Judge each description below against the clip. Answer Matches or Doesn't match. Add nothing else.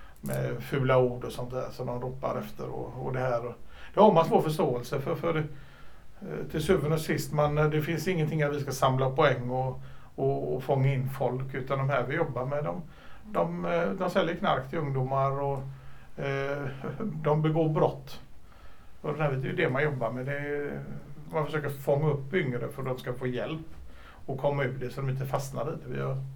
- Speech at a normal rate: Doesn't match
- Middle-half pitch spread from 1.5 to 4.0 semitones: Matches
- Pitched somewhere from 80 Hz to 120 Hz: Doesn't match